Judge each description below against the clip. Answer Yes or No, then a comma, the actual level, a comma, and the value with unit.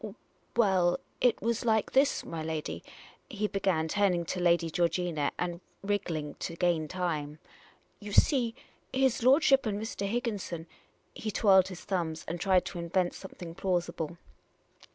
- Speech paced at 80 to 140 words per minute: No, average, 160 wpm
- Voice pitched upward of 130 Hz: Yes, medium, 185 Hz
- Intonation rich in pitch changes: No, average, 3.6 semitones